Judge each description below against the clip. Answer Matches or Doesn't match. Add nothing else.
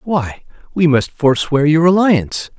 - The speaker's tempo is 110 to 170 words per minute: Matches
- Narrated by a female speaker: Doesn't match